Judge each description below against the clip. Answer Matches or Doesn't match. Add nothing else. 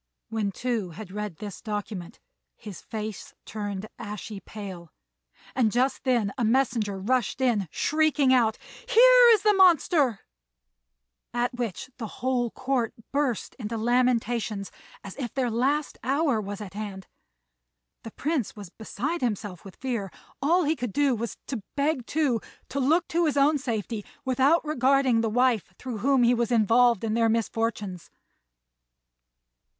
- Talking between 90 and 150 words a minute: Matches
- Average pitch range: Matches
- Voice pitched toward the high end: Matches